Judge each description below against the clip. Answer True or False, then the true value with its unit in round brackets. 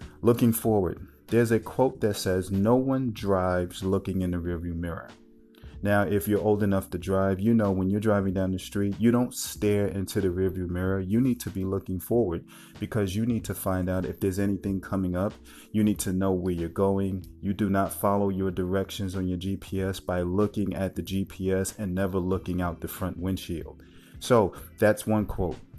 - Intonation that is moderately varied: False (2.0 semitones)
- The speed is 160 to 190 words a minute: False (200 wpm)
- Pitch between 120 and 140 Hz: False (95 Hz)